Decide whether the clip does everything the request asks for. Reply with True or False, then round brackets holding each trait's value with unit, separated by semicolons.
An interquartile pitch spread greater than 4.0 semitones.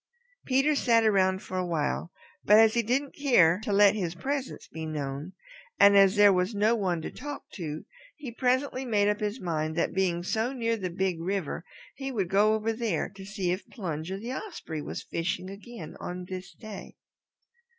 True (4.4 semitones)